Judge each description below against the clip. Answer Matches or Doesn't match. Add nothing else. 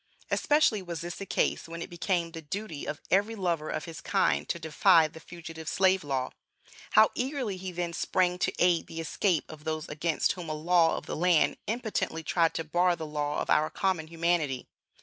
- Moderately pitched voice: Matches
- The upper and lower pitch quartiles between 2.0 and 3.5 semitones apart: Matches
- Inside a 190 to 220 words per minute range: Matches